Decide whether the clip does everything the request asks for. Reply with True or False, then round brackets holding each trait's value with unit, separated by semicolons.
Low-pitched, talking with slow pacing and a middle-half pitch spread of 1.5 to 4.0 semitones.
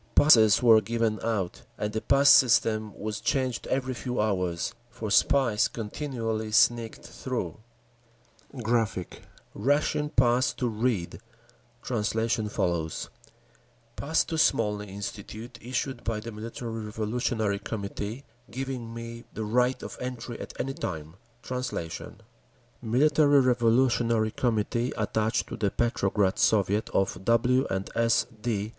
True (115 Hz; 125 wpm; 2.8 semitones)